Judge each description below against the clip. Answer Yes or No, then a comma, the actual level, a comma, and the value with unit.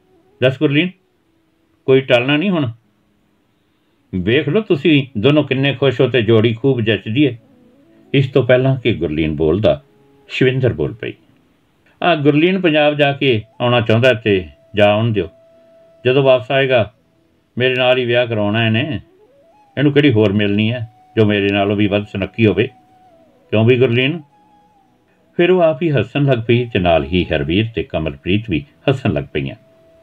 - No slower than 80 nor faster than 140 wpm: No, average, 155 wpm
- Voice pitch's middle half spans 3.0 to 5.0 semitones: No, wide, 5.6 semitones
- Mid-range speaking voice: No, low, 125 Hz